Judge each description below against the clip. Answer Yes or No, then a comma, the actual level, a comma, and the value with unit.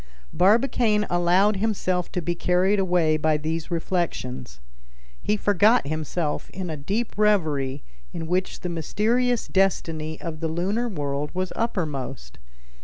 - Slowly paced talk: Yes, slow, 130 wpm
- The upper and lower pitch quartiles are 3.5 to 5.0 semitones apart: Yes, average, 4.6 semitones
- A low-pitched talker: No, medium, 175 Hz